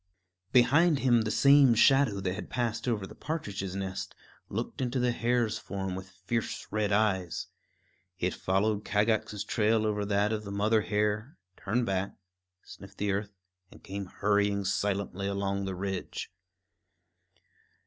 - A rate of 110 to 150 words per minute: Yes, average, 145 wpm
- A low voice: Yes, low, 105 Hz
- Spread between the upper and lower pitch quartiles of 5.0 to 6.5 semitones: No, average, 2.7 semitones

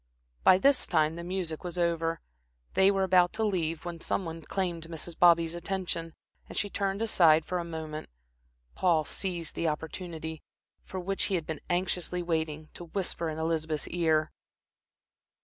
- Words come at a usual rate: Yes, average, 165 wpm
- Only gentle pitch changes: Yes, narrow, 2.3 semitones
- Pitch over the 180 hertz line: No, medium, 170 Hz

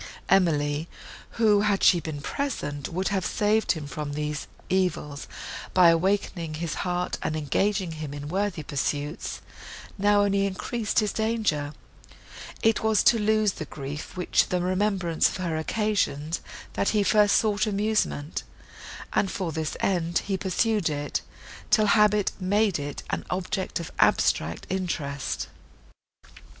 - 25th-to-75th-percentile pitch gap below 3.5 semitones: No, average, 5.0 semitones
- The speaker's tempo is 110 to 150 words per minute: Yes, slow, 135 wpm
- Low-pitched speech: No, medium, 185 Hz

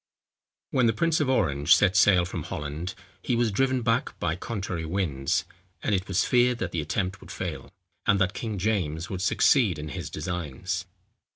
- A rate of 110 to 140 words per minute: No, average, 180 wpm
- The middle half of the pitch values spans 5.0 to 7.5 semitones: Yes, average, 5.3 semitones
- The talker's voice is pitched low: Yes, very low, 95 Hz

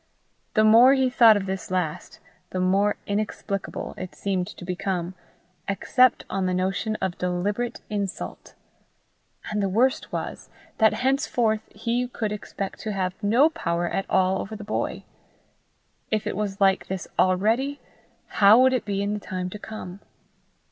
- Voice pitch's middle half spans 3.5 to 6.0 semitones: No, average, 2.9 semitones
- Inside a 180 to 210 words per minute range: No, average, 155 wpm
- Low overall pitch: No, high, 205 Hz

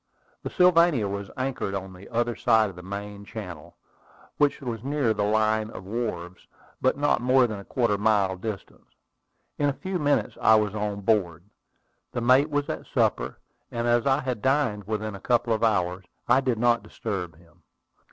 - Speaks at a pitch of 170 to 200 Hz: No, low, 110 Hz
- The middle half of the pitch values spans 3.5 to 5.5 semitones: Yes, average, 4.2 semitones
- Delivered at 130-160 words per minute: No, average, 190 wpm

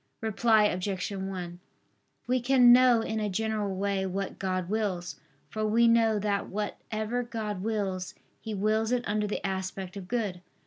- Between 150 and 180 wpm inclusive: Yes, average, 160 wpm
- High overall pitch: Yes, high, 210 Hz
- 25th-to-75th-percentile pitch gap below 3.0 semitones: Yes, narrow, 2.6 semitones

